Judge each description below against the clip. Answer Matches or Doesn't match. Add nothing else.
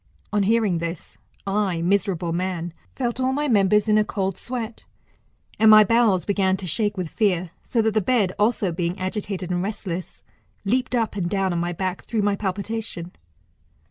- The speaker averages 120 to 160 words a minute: Doesn't match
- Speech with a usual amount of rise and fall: Matches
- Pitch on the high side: Matches